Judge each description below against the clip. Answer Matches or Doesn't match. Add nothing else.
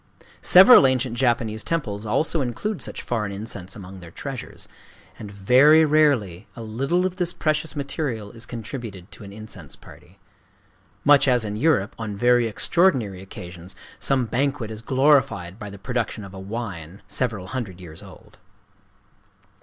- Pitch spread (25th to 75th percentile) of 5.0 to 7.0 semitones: Matches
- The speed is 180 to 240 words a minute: Doesn't match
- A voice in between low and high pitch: Doesn't match